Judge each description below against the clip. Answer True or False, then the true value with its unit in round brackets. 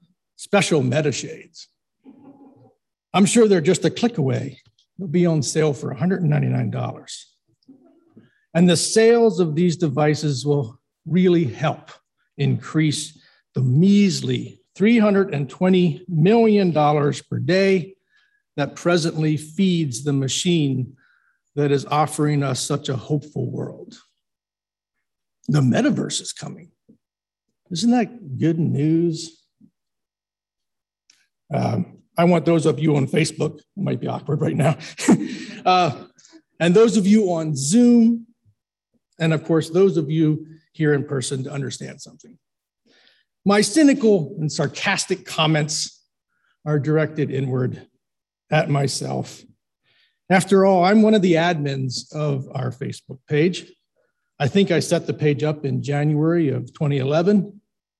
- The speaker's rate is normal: False (120 wpm)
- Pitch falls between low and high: True (160 Hz)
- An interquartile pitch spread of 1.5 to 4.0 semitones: False (4.6 semitones)